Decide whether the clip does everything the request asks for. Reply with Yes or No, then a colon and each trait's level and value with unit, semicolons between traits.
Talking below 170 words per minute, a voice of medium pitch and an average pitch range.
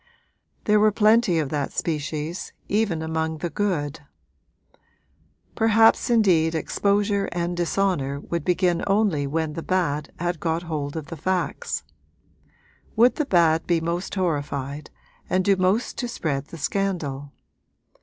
Yes: slow, 135 wpm; medium, 170 Hz; average, 4.2 semitones